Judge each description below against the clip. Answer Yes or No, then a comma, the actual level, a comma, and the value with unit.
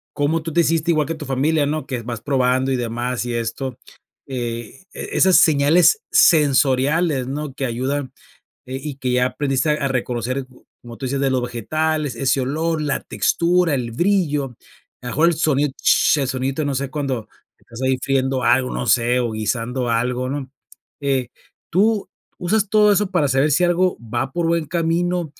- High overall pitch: No, low, 135 Hz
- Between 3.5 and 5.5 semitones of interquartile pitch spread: Yes, average, 3.9 semitones